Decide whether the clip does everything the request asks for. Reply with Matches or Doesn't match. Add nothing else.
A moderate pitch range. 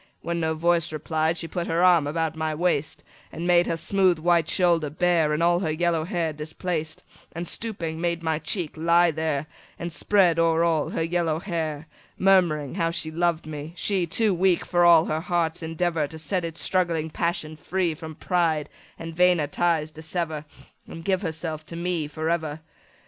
Doesn't match